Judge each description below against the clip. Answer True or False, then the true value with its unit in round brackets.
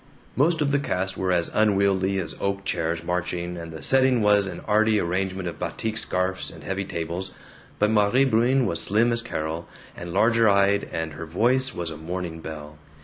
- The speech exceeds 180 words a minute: True (190 wpm)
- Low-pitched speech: True (95 Hz)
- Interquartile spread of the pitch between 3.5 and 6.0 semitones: True (4.3 semitones)